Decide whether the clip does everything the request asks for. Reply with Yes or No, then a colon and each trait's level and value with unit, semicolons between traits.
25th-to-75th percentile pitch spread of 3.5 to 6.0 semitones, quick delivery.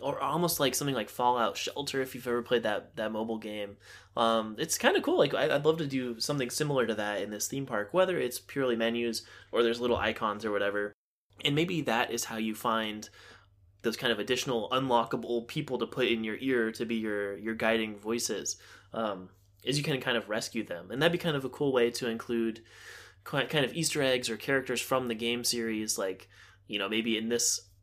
No: average, 3.1 semitones; fast, 220 wpm